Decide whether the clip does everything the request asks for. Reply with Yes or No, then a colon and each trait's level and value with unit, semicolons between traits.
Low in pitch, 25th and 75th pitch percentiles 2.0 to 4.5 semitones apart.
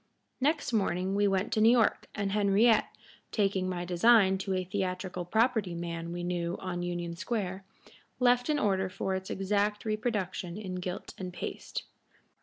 No: high, 190 Hz; average, 3.0 semitones